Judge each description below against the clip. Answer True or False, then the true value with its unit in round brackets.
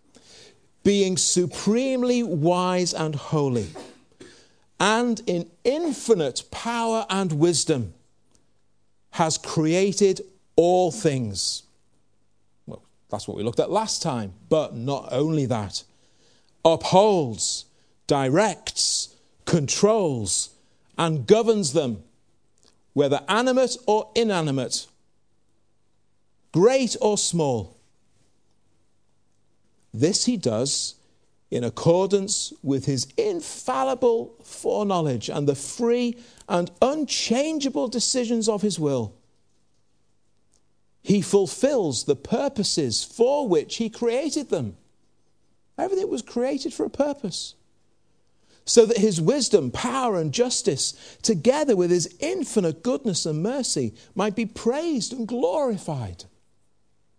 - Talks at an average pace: False (95 wpm)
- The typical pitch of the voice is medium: True (175 Hz)